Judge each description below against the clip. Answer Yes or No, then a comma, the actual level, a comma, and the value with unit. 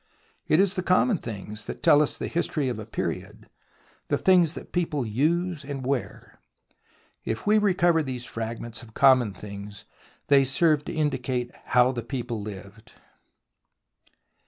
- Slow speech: No, average, 150 wpm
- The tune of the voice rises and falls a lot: Yes, wide, 6.1 semitones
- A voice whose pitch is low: Yes, low, 130 Hz